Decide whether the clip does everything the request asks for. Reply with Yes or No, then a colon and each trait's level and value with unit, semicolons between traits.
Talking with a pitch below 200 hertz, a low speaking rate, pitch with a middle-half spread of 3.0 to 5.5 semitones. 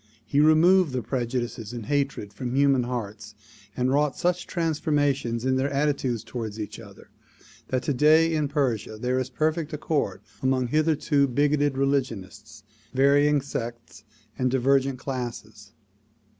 Yes: low, 135 Hz; slow, 130 wpm; average, 3.4 semitones